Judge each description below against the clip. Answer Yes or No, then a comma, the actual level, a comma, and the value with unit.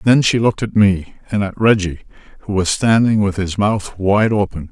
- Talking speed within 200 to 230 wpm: Yes, fast, 205 wpm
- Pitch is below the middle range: Yes, low, 100 Hz